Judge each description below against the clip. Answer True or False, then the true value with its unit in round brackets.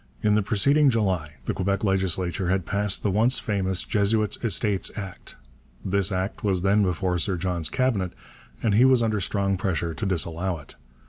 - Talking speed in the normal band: True (175 wpm)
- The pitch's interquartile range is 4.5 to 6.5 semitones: False (2.5 semitones)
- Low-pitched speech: True (95 Hz)